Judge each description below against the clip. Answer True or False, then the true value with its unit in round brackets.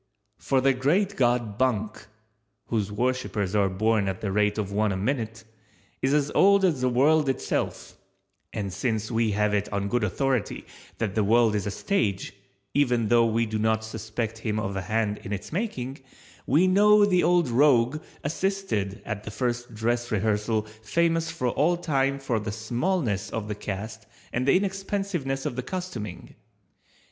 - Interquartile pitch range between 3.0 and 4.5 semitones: False (4.9 semitones)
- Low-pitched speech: True (115 Hz)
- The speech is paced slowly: False (170 wpm)